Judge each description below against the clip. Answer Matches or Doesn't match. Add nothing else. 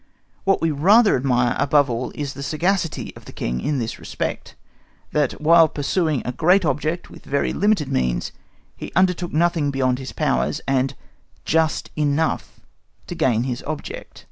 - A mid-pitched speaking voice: Matches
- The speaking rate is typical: Matches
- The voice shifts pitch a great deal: Doesn't match